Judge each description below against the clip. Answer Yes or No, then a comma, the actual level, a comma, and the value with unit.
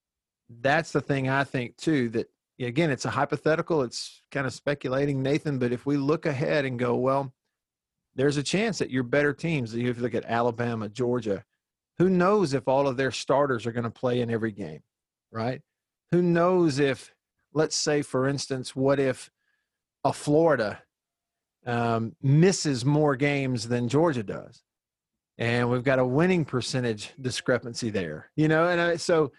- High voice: No, low, 135 Hz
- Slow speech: No, average, 165 wpm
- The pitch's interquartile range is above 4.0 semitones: No, average, 3.6 semitones